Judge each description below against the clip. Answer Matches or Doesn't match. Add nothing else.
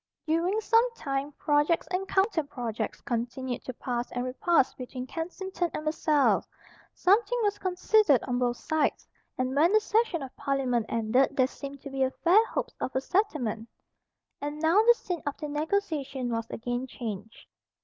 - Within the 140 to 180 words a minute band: Matches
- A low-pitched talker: Doesn't match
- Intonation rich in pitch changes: Matches